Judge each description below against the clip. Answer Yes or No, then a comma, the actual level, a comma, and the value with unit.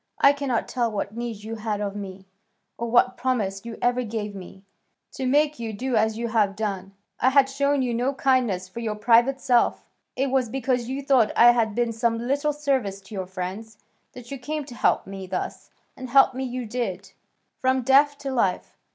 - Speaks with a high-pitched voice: Yes, high, 235 Hz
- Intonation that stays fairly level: No, average, 3.8 semitones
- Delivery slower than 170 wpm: No, fast, 205 wpm